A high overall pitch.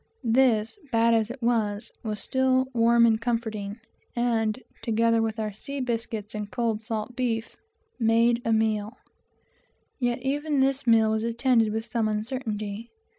Yes: high, 230 Hz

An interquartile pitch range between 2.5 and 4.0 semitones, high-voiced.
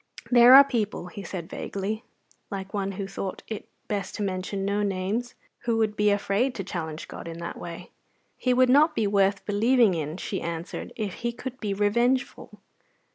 Yes: average, 3.7 semitones; high, 205 Hz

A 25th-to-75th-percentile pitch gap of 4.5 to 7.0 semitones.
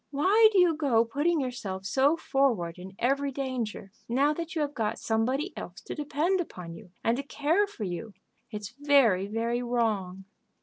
Yes: wide, 5.5 semitones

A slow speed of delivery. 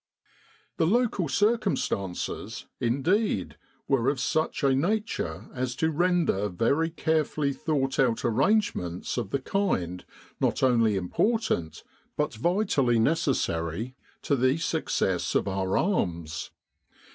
Yes: slow, 110 wpm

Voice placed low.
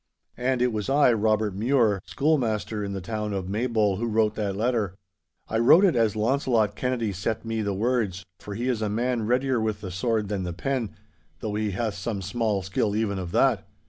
Yes: low, 110 Hz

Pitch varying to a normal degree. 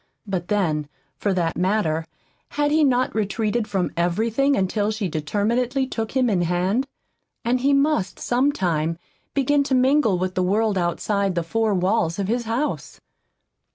No: wide, 5.7 semitones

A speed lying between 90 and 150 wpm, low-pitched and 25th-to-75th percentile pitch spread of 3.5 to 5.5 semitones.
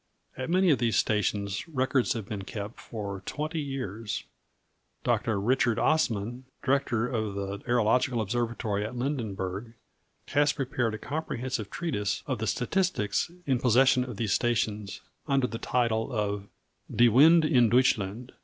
Yes: average, 140 wpm; low, 120 Hz; average, 3.9 semitones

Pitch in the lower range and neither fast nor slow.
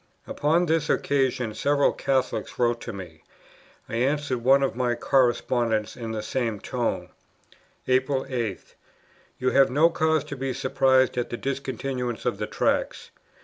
Yes: low, 130 Hz; average, 145 wpm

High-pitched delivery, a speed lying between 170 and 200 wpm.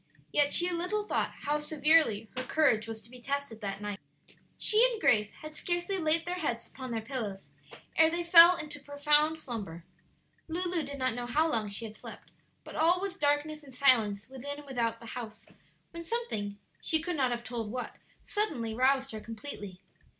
Yes: very high, 280 Hz; average, 185 wpm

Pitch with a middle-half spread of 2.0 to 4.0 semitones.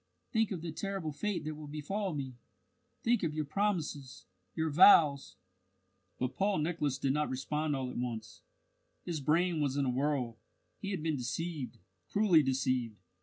No: average, 4.6 semitones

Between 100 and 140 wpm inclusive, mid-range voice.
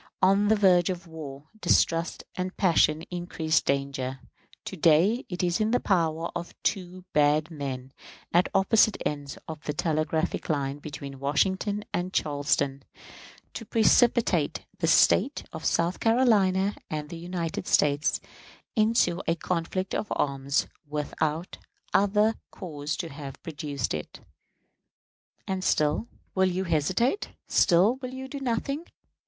Yes: slow, 135 wpm; medium, 170 Hz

